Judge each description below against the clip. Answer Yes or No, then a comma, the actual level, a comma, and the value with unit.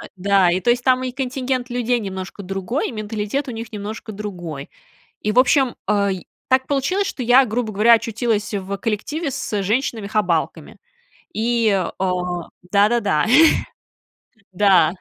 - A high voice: Yes, high, 215 Hz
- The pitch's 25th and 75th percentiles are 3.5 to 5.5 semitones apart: Yes, average, 3.9 semitones